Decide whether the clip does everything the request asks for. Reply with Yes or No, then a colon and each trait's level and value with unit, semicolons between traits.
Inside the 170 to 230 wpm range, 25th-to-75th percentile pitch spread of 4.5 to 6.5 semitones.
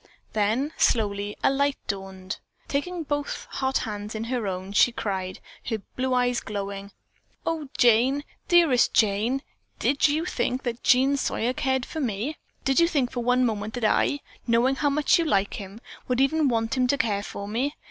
Yes: average, 180 wpm; average, 4.8 semitones